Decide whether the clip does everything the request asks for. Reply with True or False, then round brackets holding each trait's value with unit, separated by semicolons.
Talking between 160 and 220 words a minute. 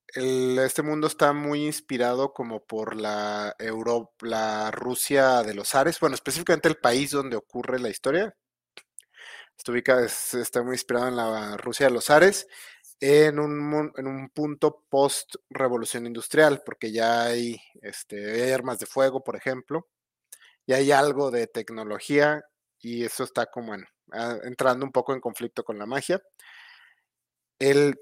False (150 wpm)